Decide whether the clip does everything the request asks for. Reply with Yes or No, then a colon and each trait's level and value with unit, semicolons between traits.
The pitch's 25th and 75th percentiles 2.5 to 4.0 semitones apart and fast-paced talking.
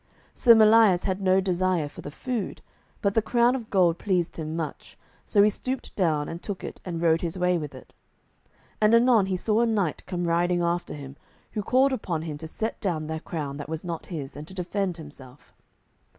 No: average, 4.6 semitones; fast, 210 wpm